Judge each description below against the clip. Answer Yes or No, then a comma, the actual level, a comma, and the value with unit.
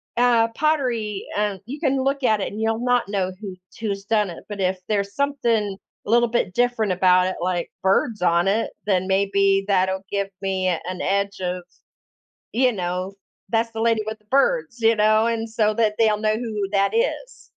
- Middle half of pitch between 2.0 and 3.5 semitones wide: Yes, average, 3.2 semitones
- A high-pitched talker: Yes, high, 210 Hz